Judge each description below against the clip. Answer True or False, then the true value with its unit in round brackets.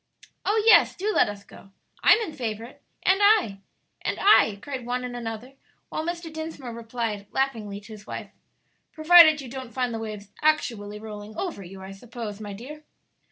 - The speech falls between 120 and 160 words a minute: False (185 wpm)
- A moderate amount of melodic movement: False (6.6 semitones)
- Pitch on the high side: True (240 Hz)